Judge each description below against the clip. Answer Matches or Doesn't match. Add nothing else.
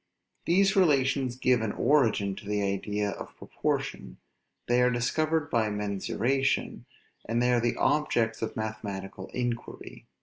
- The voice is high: Doesn't match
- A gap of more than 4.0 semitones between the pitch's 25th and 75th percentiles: Matches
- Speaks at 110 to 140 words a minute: Matches